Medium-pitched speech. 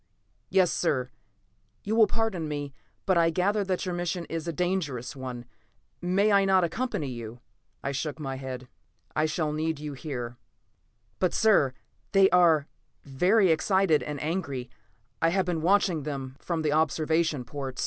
Yes: medium, 160 Hz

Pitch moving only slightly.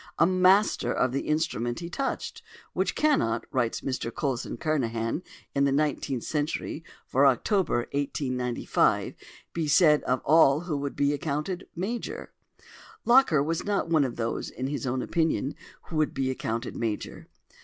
No: average, 4.5 semitones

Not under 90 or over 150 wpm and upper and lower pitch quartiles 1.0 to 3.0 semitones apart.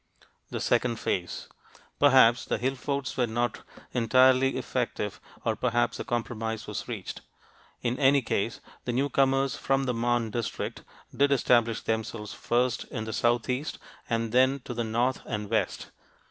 Yes: average, 145 wpm; narrow, 2.5 semitones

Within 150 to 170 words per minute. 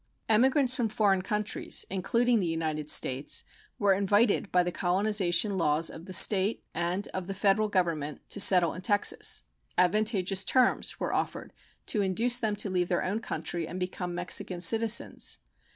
Yes: average, 160 wpm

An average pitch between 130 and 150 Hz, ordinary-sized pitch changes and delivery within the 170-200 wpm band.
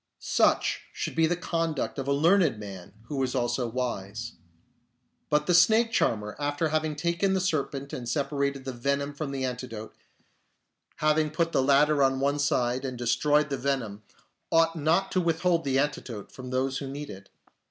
Yes: medium, 140 Hz; average, 3.7 semitones; average, 175 wpm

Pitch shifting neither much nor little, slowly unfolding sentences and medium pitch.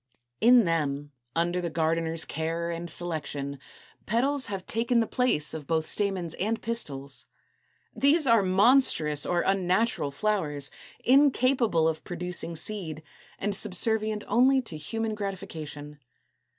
No: wide, 5.9 semitones; slow, 125 wpm; medium, 180 Hz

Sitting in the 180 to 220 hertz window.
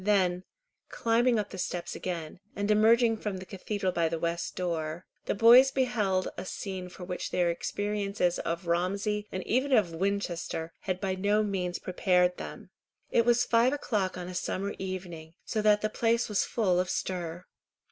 Yes: high, 190 Hz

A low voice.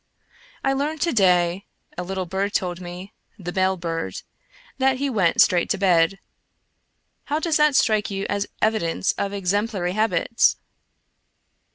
No: high, 195 Hz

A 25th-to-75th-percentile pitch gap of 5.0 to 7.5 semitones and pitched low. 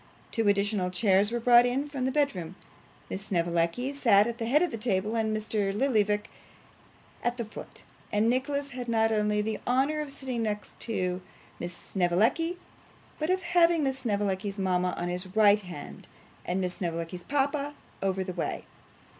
No: wide, 5.5 semitones; high, 215 Hz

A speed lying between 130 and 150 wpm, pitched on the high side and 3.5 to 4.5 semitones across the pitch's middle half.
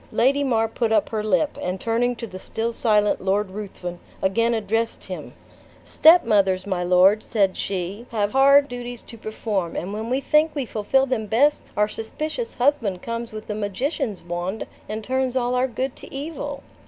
No: average, 180 wpm; high, 225 Hz; average, 4.1 semitones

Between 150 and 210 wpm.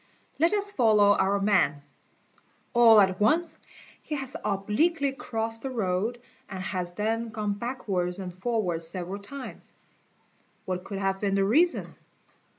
No: average, 140 wpm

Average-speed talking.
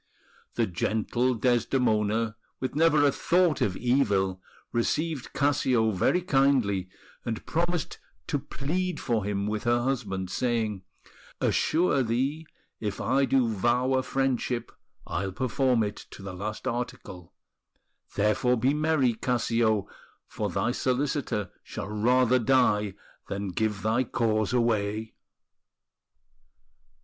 No: slow, 120 wpm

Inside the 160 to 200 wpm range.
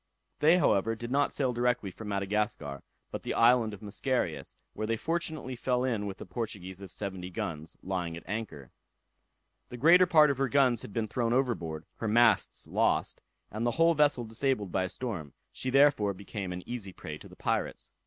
Yes: average, 190 wpm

